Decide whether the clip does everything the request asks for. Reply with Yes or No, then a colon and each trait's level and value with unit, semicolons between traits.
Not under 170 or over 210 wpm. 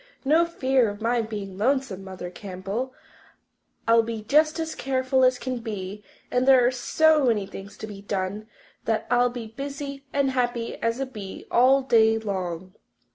Yes: average, 175 wpm